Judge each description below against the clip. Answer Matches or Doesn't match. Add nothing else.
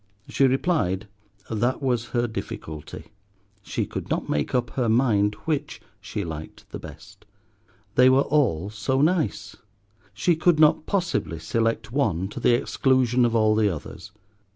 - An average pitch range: Matches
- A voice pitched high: Doesn't match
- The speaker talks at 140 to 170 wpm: Matches